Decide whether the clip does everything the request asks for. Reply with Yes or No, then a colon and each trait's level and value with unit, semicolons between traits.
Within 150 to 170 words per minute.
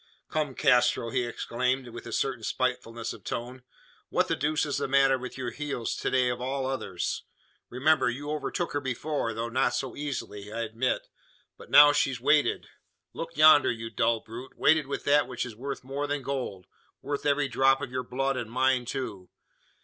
No: average, 190 wpm